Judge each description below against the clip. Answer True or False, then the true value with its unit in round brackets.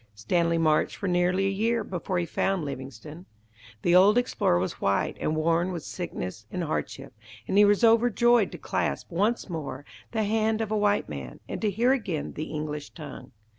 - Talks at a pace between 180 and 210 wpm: True (185 wpm)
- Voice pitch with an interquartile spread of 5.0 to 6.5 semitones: True (5.4 semitones)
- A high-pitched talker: False (180 Hz)